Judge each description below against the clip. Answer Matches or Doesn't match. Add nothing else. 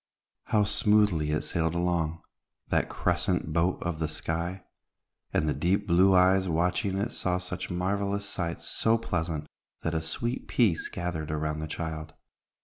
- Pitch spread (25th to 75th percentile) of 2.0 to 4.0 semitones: Matches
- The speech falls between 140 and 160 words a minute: Matches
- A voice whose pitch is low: Matches